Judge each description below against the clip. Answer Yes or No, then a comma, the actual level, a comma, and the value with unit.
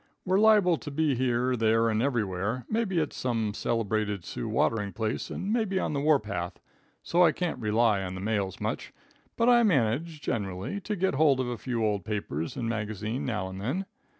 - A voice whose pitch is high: No, low, 120 Hz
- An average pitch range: No, wide, 7.0 semitones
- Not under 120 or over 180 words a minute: No, average, 190 wpm